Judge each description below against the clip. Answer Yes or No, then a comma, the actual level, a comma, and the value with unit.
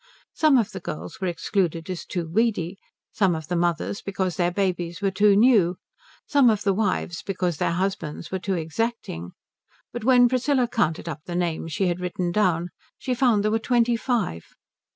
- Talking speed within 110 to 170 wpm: No, average, 185 wpm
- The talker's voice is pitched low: No, high, 190 Hz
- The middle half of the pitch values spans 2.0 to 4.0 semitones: No, average, 4.4 semitones